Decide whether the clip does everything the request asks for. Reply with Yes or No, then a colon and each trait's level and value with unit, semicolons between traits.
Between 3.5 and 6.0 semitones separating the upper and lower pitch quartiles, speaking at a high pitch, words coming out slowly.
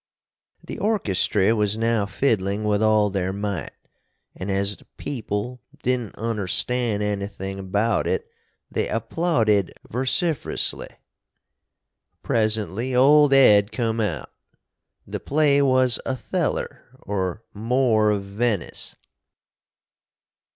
No: average, 3.9 semitones; low, 110 Hz; slow, 100 wpm